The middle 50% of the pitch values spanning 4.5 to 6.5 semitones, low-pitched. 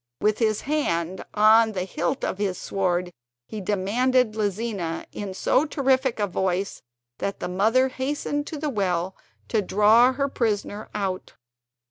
No: average, 5.0 semitones; high, 210 Hz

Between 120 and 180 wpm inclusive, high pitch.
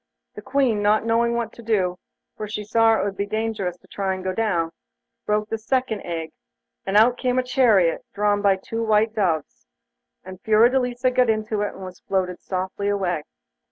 No: average, 190 wpm; high, 210 Hz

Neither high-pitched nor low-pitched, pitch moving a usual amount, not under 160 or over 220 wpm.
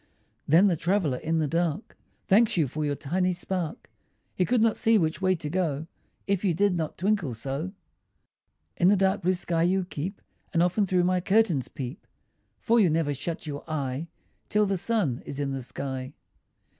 Yes: medium, 175 Hz; average, 4.5 semitones; average, 185 wpm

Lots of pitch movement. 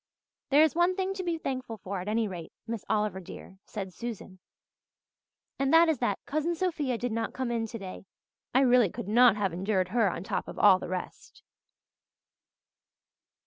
Yes: wide, 5.9 semitones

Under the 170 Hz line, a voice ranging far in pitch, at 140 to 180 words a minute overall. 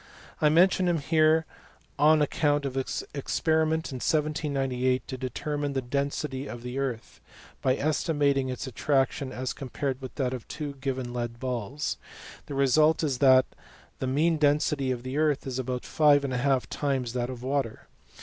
No: low, 135 Hz; narrow, 2.6 semitones; average, 170 wpm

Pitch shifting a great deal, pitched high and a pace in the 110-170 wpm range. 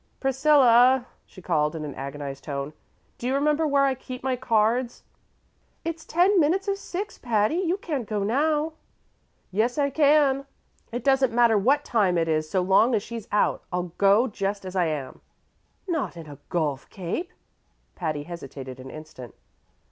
Yes: wide, 8.6 semitones; high, 230 Hz; average, 165 wpm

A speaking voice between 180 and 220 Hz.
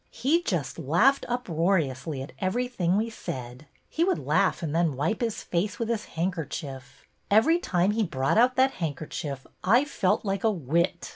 Yes: medium, 185 Hz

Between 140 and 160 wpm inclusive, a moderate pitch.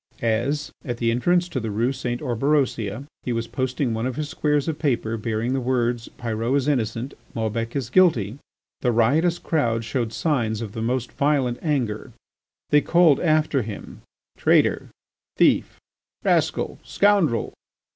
No: average, 150 wpm; low, 125 Hz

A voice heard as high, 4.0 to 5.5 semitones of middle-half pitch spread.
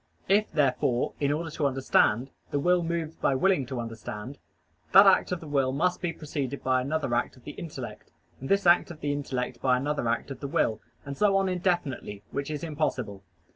No: medium, 145 Hz; average, 4.7 semitones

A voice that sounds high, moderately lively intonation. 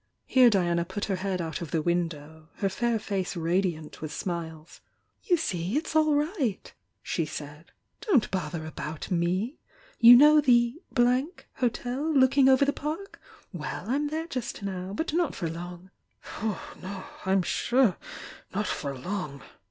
No: high, 195 Hz; wide, 7.4 semitones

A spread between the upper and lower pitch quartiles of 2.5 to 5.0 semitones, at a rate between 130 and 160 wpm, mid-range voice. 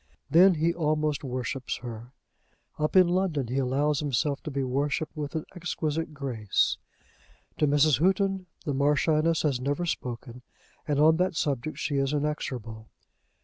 Yes: average, 3.1 semitones; average, 145 wpm; medium, 150 Hz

